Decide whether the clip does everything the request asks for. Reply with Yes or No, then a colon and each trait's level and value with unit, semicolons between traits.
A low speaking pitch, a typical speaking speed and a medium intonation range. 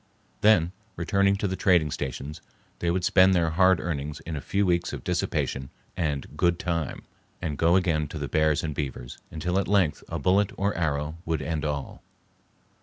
Yes: very low, 80 Hz; average, 180 wpm; average, 3.6 semitones